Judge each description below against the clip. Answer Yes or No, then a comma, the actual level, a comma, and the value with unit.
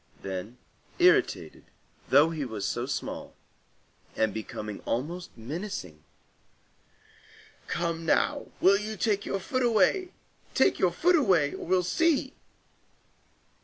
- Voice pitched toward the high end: No, medium, 170 Hz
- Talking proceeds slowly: Yes, slow, 115 wpm